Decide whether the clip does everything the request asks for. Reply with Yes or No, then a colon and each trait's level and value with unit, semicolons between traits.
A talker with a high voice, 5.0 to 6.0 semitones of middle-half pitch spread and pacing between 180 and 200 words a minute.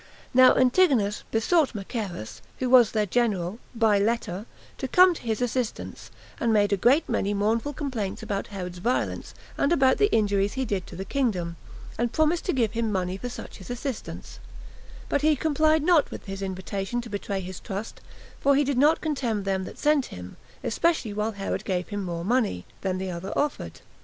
Yes: high, 225 Hz; average, 5.3 semitones; average, 185 wpm